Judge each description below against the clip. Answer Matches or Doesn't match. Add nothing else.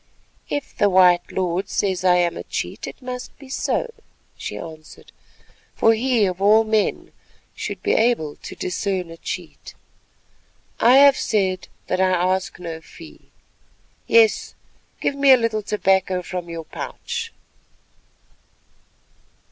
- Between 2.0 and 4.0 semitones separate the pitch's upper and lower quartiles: Doesn't match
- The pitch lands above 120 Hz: Matches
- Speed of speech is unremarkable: Doesn't match